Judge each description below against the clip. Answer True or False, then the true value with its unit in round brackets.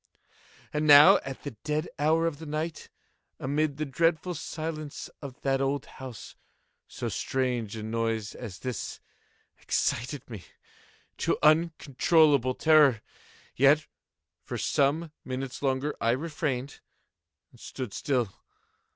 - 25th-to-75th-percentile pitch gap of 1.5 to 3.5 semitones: True (3.2 semitones)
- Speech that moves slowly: True (120 wpm)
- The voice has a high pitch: False (140 Hz)